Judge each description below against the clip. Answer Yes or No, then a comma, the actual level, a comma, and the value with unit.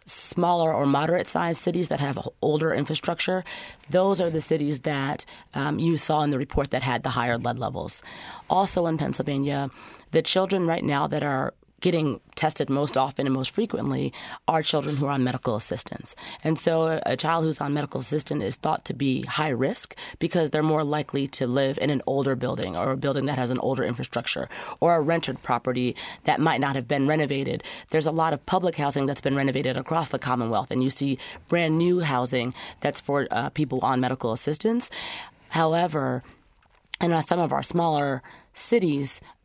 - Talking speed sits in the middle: Yes, average, 190 wpm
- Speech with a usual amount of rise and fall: Yes, average, 3.6 semitones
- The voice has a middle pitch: Yes, medium, 145 Hz